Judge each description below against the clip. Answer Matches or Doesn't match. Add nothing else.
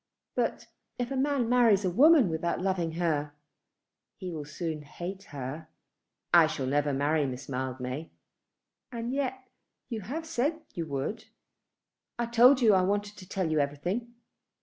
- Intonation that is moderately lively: Doesn't match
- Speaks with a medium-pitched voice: Matches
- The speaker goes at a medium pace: Matches